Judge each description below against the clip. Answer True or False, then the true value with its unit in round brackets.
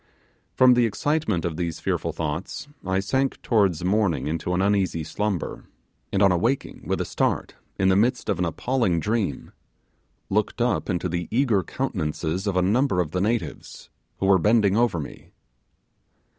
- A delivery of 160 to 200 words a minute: True (165 wpm)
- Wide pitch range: False (4.7 semitones)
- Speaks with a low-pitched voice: True (95 Hz)